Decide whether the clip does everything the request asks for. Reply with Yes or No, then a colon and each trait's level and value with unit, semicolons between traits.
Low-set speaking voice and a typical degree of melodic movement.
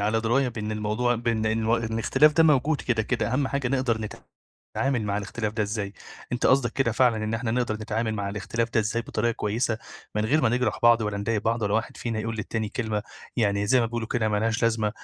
No: low, 115 Hz; narrow, 2.1 semitones